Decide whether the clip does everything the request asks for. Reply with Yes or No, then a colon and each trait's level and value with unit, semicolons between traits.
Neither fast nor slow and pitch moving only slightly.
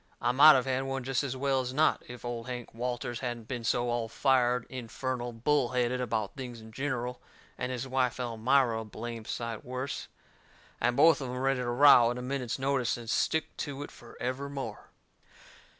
Yes: average, 190 wpm; narrow, 2.0 semitones